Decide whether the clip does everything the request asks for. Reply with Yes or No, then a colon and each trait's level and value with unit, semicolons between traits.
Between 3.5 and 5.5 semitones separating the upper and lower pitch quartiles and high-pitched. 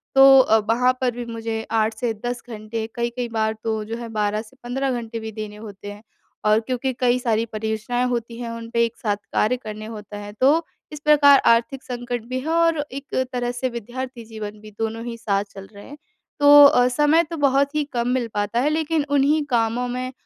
No: average, 2.8 semitones; high, 235 Hz